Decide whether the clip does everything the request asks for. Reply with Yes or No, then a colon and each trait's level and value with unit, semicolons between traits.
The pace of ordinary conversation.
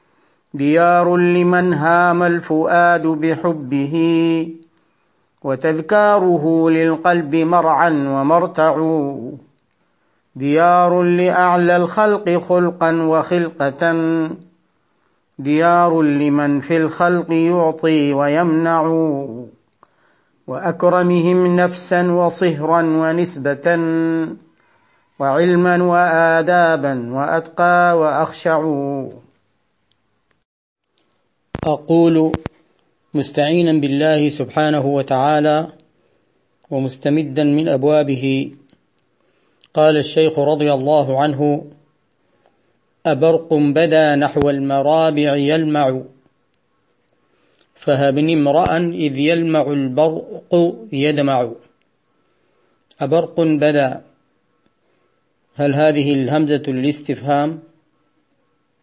No: slow, 60 wpm